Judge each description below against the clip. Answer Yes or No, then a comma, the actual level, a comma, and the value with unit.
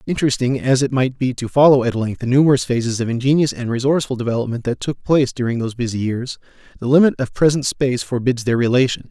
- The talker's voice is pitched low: Yes, low, 125 Hz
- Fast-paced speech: Yes, fast, 210 wpm